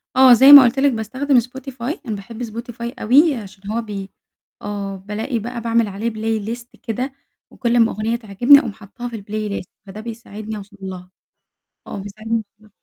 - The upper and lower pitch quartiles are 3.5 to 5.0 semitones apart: No, average, 2.8 semitones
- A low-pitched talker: No, high, 225 Hz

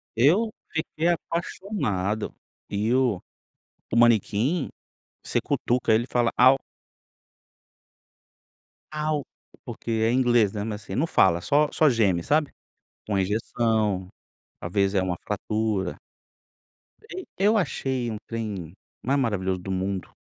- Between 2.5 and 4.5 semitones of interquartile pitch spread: No, average, 5.3 semitones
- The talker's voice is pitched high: No, low, 115 Hz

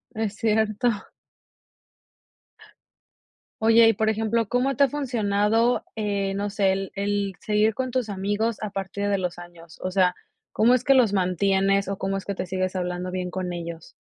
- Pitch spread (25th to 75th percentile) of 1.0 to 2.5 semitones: No, average, 2.9 semitones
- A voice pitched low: No, high, 200 Hz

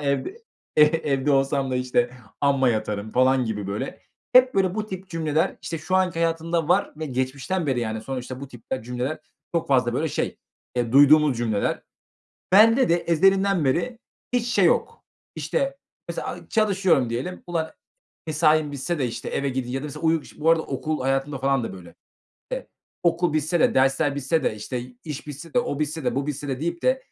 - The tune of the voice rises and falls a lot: No, average, 4.6 semitones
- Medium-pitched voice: Yes, medium, 150 Hz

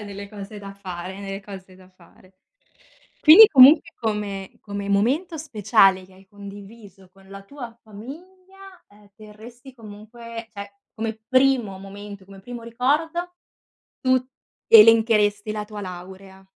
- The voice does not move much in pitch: No, average, 3.6 semitones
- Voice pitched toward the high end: Yes, high, 210 Hz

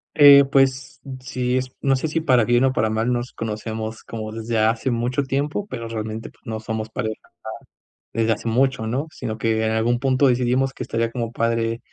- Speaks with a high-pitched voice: No, low, 120 Hz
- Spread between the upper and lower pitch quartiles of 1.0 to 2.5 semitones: No, average, 2.9 semitones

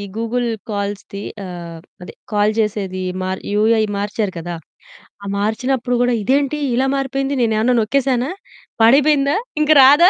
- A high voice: Yes, high, 230 Hz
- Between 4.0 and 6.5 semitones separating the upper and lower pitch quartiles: Yes, average, 4.8 semitones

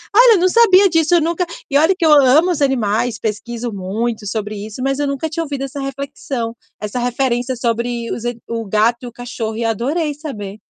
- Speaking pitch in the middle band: No, very high, 250 Hz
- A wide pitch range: No, average, 4.7 semitones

